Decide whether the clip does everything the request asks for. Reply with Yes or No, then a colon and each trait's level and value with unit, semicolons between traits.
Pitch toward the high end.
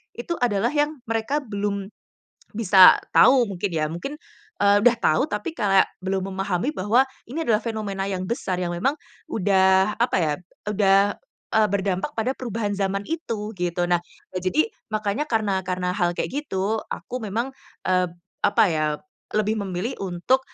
Yes: high, 205 Hz